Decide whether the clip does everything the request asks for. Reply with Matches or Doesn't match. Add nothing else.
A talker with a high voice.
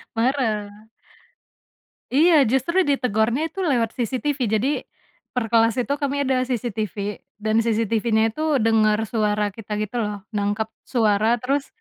Matches